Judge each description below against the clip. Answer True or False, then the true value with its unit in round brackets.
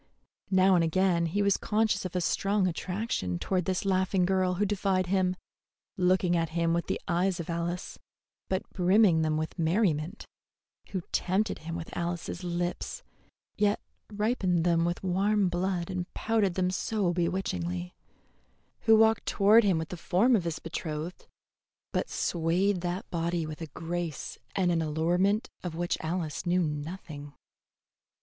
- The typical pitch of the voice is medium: True (180 Hz)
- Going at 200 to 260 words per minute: False (155 wpm)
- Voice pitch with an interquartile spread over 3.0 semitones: False (2.5 semitones)